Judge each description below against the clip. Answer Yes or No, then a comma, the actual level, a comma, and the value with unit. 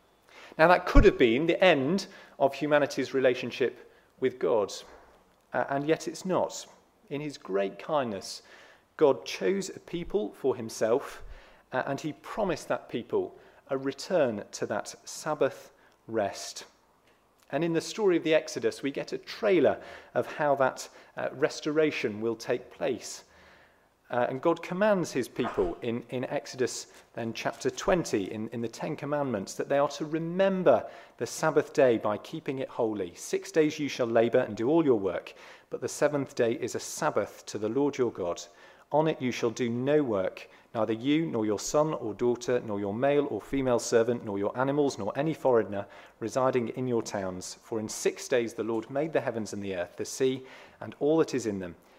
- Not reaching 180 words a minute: No, average, 185 wpm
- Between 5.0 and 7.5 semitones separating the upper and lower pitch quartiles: Yes, wide, 5.5 semitones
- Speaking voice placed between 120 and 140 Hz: Yes, low, 135 Hz